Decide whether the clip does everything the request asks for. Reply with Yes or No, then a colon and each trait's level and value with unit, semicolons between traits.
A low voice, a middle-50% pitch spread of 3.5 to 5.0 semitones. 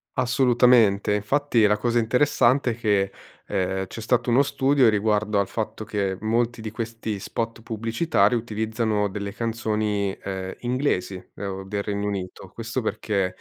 No: low, 110 Hz; average, 2.7 semitones